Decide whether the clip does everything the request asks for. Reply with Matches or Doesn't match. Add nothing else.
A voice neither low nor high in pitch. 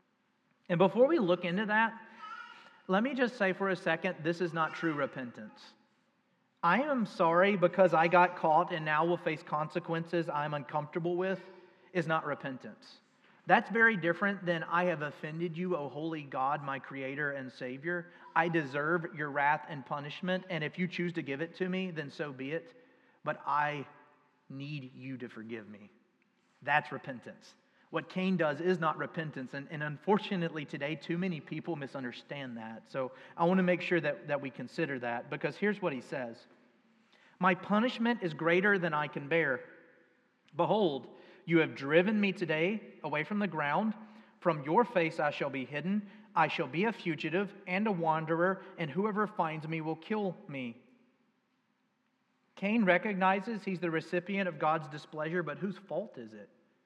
Matches